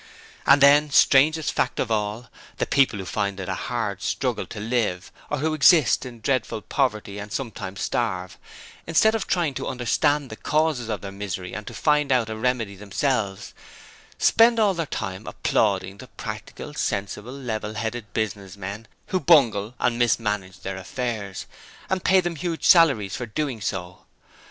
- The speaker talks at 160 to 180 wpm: Yes, average, 165 wpm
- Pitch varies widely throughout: Yes, wide, 5.9 semitones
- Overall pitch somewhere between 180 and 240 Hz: No, low, 115 Hz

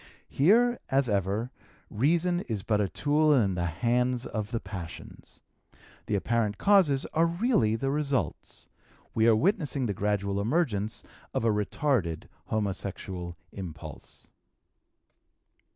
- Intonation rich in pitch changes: Yes, wide, 6.4 semitones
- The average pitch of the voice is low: Yes, low, 115 Hz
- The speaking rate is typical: No, slow, 120 wpm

